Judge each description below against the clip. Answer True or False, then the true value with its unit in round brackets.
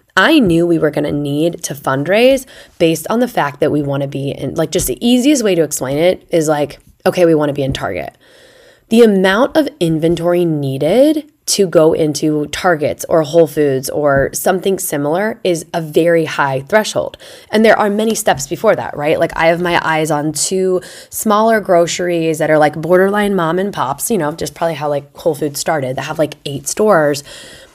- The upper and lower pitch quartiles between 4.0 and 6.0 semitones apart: True (4.5 semitones)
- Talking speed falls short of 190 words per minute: False (195 wpm)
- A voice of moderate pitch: True (165 Hz)